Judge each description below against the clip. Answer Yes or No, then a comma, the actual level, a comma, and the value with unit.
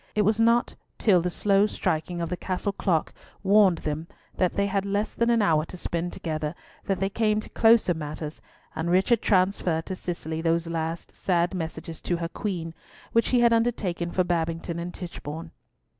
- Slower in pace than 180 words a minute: No, average, 185 wpm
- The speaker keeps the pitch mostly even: No, average, 3.5 semitones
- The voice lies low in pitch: No, medium, 180 Hz